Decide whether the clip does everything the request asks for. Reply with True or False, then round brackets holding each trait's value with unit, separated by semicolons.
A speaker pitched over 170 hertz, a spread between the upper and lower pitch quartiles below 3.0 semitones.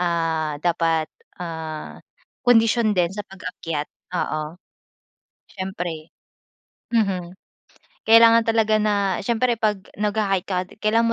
False (190 Hz; 4.5 semitones)